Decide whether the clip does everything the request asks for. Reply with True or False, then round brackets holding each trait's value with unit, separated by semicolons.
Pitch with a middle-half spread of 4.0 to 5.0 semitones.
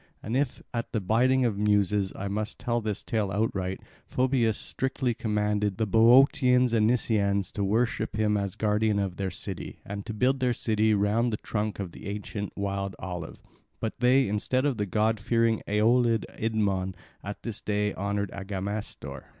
False (2.5 semitones)